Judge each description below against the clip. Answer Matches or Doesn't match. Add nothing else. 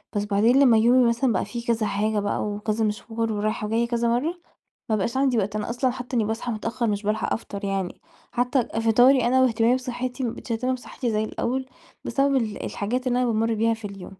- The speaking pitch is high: Matches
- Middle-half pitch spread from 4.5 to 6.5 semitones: Doesn't match